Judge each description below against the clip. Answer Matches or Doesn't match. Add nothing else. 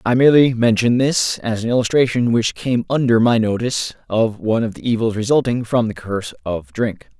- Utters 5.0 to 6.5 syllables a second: Matches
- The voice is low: Matches